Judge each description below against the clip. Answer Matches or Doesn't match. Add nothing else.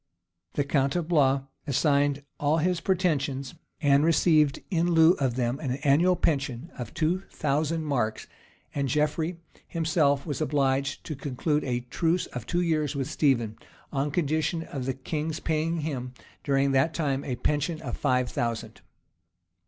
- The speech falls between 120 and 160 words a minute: Matches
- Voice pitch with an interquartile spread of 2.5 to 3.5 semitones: Matches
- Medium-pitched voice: Matches